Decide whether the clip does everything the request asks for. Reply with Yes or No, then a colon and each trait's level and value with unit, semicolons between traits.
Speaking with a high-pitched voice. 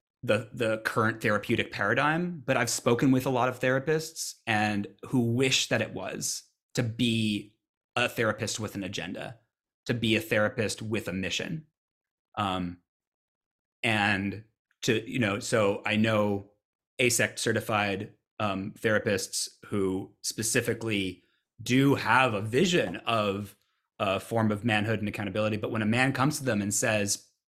No: low, 110 Hz